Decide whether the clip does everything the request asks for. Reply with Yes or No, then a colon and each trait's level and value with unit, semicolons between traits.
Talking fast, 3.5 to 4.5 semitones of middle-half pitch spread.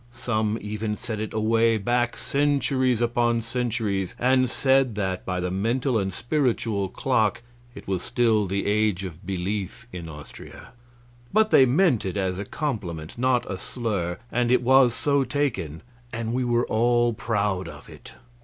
No: average, 160 wpm; average, 4.0 semitones